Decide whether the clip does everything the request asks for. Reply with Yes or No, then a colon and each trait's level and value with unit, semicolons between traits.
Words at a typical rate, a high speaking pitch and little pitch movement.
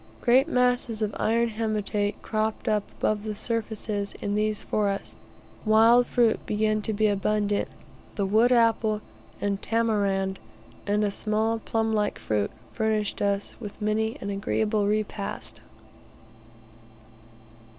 No: slow, 125 wpm; high, 215 Hz; narrow, 1.5 semitones